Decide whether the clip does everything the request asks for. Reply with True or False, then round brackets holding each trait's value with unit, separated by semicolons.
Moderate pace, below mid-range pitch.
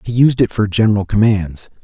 True (195 wpm; 105 Hz)